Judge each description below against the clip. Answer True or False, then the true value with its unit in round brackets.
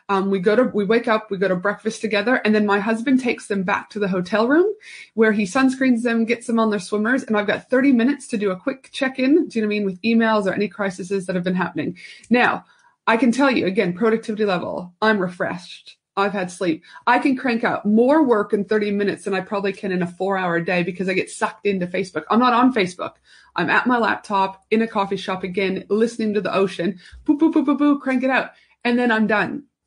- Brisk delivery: True (245 wpm)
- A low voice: False (215 Hz)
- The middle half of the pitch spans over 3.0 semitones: True (3.8 semitones)